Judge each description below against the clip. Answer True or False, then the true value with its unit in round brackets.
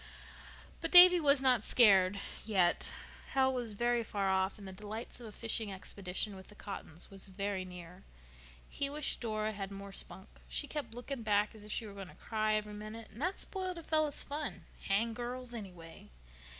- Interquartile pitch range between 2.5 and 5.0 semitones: True (4.0 semitones)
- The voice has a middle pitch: False (215 Hz)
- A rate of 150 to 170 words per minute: False (185 wpm)